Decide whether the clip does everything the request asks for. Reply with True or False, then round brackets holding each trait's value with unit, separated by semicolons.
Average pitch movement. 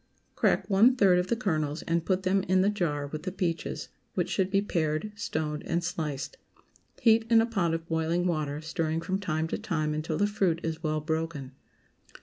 True (3.8 semitones)